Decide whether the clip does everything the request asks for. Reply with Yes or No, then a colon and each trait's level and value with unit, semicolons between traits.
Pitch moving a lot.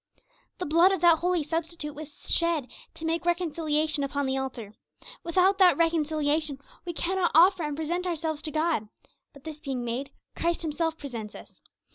No: average, 2.8 semitones